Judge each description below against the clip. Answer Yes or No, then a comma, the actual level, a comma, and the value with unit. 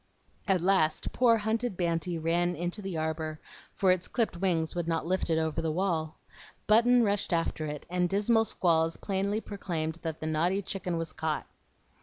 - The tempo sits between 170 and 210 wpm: Yes, average, 175 wpm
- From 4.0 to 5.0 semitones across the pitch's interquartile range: No, average, 3.5 semitones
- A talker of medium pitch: Yes, medium, 175 Hz